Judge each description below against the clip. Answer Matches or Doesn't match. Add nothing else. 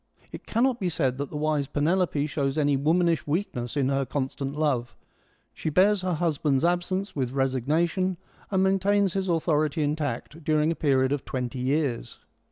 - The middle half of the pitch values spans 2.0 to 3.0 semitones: Doesn't match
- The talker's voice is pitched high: Doesn't match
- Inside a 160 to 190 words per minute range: Matches